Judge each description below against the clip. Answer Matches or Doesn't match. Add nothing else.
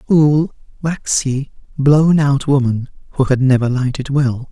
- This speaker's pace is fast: Doesn't match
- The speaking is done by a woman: Matches